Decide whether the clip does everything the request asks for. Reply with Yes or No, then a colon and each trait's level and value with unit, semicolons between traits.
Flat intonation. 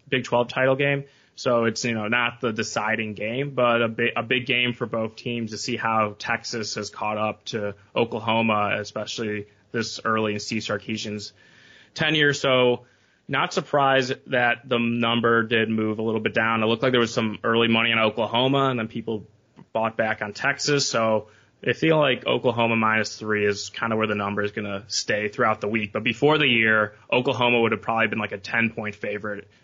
Yes: narrow, 2.2 semitones